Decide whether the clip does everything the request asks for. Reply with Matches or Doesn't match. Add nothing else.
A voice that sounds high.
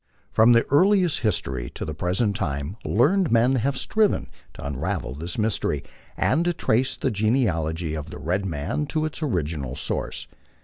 Doesn't match